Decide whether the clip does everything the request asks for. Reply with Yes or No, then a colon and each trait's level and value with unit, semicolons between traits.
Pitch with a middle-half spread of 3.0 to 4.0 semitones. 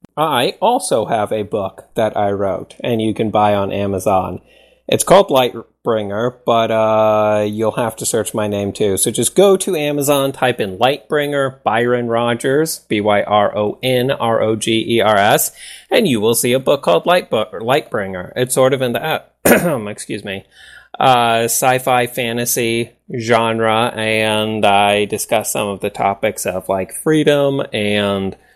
Yes: average, 3.4 semitones